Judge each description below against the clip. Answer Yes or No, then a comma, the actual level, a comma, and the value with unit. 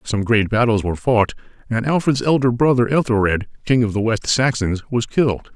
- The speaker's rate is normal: Yes, average, 185 wpm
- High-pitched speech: No, low, 115 Hz